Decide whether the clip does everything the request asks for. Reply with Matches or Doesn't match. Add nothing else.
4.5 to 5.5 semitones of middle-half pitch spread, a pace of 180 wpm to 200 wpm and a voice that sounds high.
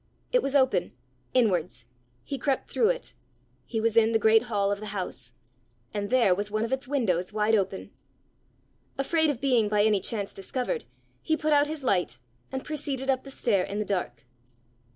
Matches